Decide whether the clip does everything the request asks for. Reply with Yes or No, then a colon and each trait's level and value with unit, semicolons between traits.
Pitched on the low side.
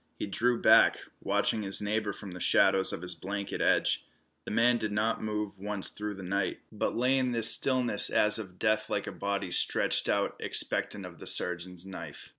Yes: low, 105 Hz